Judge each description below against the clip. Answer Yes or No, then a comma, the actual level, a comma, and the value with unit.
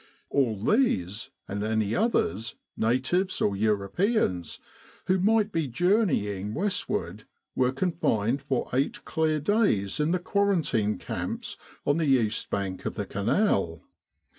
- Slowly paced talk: Yes, slow, 125 wpm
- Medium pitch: No, low, 130 Hz